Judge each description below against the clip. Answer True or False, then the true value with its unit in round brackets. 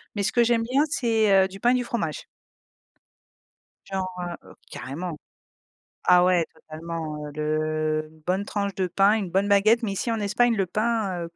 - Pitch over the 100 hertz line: True (190 Hz)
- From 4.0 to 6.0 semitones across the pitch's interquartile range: True (4.7 semitones)